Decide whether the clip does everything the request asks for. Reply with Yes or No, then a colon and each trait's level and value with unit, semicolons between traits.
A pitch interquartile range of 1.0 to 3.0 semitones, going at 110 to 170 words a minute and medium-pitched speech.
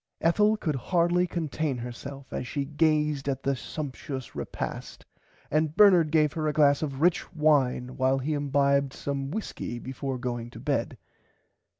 Yes: average, 2.7 semitones; average, 155 wpm; medium, 145 Hz